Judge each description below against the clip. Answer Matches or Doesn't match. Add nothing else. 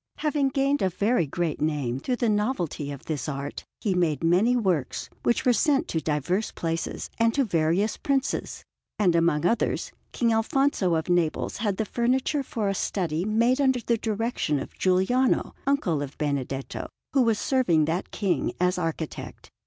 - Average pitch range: Doesn't match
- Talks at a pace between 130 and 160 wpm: Doesn't match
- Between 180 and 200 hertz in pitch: Matches